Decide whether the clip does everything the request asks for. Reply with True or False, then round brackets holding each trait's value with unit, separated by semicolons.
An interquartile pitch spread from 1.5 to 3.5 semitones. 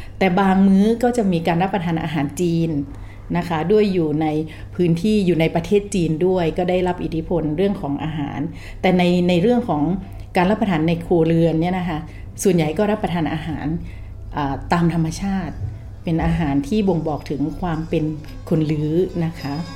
True (3.2 semitones)